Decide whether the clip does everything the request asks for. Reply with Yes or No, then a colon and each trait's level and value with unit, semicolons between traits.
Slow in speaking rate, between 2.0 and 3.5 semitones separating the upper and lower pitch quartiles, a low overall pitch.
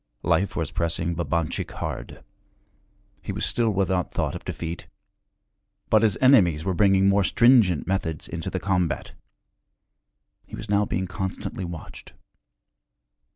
Yes: slow, 130 wpm; average, 3.1 semitones; very low, 95 Hz